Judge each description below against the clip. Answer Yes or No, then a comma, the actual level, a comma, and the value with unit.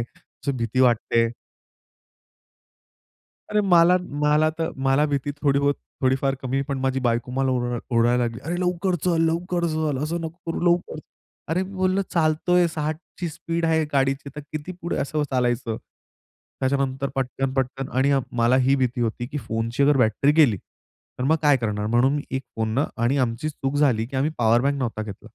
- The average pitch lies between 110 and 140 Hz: Yes, low, 135 Hz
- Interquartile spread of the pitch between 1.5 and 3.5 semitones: No, average, 4.2 semitones